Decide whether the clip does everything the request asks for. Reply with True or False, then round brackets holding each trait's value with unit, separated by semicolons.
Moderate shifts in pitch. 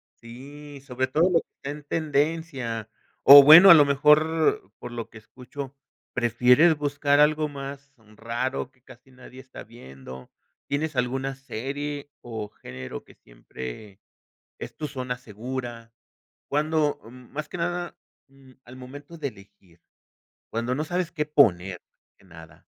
True (4.2 semitones)